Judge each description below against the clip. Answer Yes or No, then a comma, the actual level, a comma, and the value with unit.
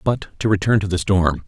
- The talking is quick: Yes, fast, 245 wpm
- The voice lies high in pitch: No, low, 100 Hz